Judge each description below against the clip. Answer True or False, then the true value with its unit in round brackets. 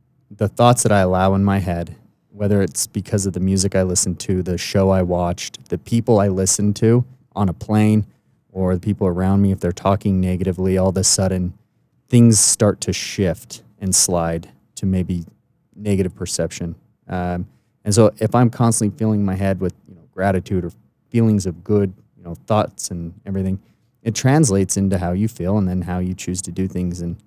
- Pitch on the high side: False (95 Hz)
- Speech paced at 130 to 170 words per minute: False (195 wpm)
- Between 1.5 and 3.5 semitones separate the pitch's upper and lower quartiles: True (2.6 semitones)